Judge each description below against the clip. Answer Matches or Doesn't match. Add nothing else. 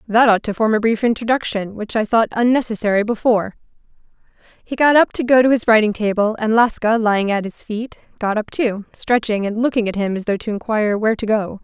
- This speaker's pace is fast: Matches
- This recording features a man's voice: Doesn't match